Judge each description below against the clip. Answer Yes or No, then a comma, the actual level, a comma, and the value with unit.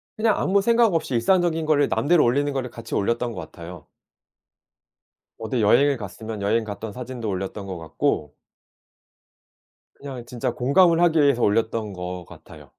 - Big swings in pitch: Yes, wide, 5.9 semitones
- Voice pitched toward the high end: No, low, 120 Hz